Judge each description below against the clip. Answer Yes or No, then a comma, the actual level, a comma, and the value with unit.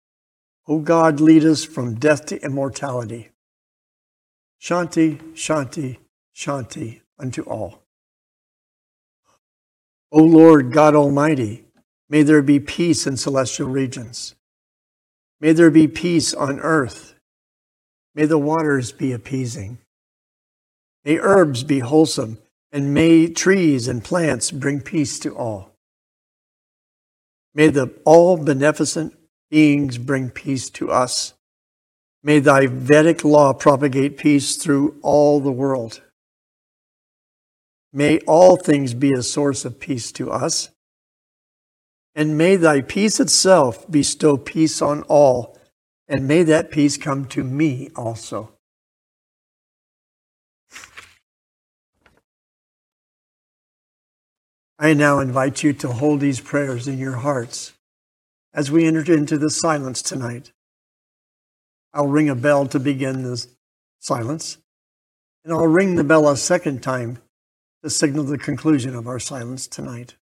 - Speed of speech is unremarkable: No, slow, 115 wpm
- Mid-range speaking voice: Yes, medium, 145 Hz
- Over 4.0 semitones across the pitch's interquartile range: No, average, 3.2 semitones